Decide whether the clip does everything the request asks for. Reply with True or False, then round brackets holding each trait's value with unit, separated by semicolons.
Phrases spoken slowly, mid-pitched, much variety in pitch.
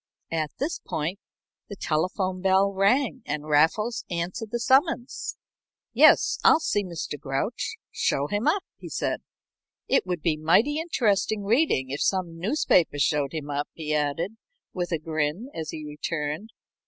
False (150 wpm; 180 Hz; 6.3 semitones)